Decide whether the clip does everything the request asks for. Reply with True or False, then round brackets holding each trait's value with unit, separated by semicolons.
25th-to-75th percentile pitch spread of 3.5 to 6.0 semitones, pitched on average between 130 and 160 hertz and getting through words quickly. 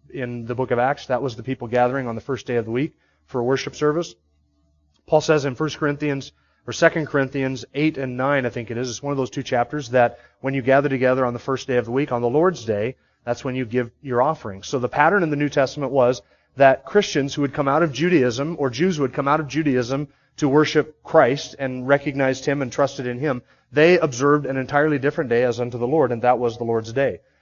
False (3.0 semitones; 135 Hz; 250 wpm)